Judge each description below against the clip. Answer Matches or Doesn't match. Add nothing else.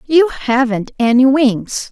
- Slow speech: Matches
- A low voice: Doesn't match